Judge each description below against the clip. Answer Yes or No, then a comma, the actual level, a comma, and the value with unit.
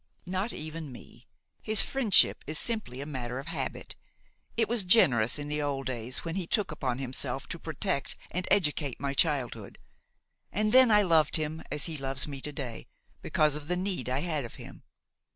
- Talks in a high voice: No, medium, 150 Hz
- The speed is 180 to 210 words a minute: Yes, average, 190 wpm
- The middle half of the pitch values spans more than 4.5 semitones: Yes, average, 5.3 semitones